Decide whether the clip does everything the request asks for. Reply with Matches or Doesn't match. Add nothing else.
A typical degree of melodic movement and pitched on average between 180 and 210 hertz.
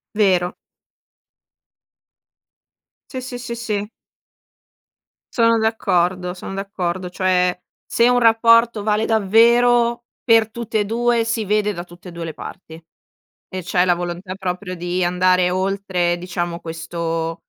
Matches